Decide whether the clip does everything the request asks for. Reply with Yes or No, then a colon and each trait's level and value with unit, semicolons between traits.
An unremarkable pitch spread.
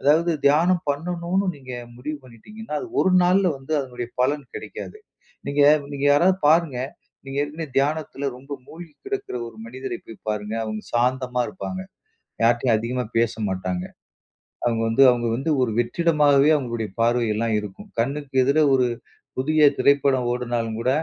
Yes: average, 4.5 semitones